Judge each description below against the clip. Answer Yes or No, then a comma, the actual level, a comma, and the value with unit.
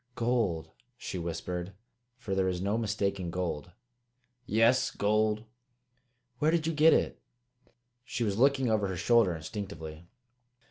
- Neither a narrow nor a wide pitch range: Yes, average, 4.5 semitones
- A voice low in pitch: Yes, low, 105 Hz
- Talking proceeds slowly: Yes, slow, 130 wpm